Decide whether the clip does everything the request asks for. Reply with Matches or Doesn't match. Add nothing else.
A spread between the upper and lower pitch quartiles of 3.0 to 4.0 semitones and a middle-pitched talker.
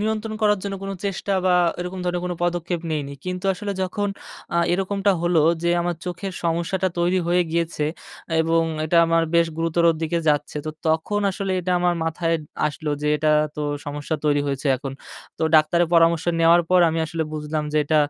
Doesn't match